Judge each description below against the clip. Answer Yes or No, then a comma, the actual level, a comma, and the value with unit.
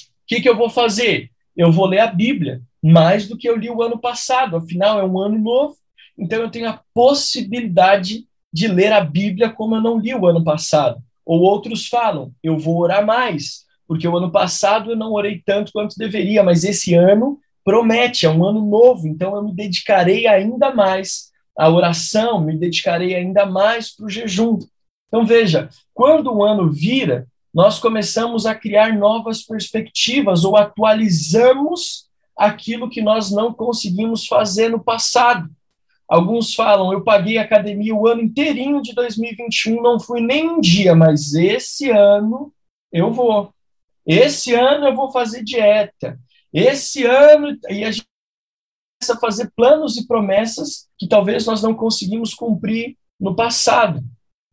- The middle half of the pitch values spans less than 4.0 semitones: Yes, average, 3.5 semitones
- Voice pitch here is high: Yes, high, 220 Hz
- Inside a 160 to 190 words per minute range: Yes, average, 165 wpm